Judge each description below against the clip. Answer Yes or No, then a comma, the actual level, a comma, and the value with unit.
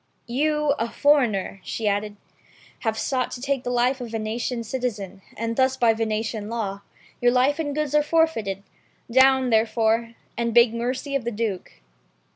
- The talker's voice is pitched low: No, high, 235 Hz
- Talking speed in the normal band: Yes, average, 170 wpm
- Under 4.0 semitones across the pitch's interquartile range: Yes, average, 3.1 semitones